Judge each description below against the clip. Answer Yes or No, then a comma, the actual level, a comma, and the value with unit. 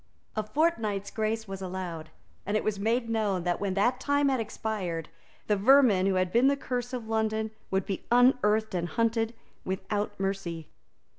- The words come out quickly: No, average, 170 wpm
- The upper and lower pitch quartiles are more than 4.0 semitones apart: No, average, 3.2 semitones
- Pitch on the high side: Yes, high, 215 Hz